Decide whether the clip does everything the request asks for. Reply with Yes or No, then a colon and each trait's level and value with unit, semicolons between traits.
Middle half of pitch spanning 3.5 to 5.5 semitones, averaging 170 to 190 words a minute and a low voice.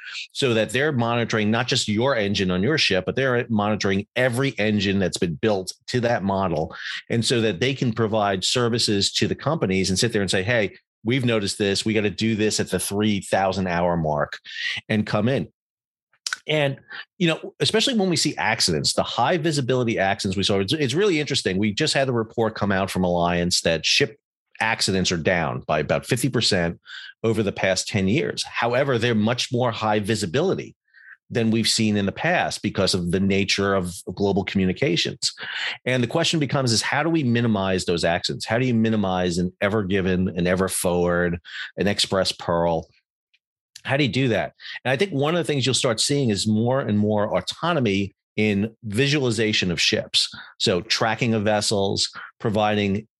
Yes: average, 4.1 semitones; average, 185 wpm; low, 110 Hz